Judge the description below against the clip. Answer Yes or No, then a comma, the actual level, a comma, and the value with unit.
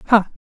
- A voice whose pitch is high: Yes, high, 210 Hz